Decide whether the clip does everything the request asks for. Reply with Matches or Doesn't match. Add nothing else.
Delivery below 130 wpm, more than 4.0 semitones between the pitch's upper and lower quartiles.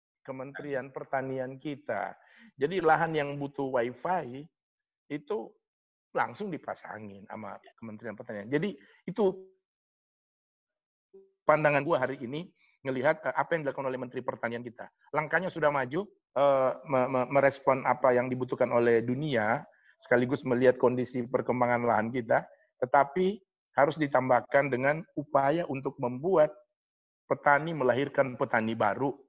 Doesn't match